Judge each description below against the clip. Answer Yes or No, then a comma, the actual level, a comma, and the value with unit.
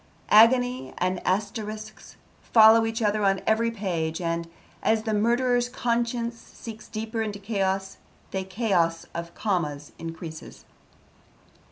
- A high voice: Yes, high, 215 Hz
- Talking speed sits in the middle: No, slow, 120 wpm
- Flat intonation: No, average, 3.7 semitones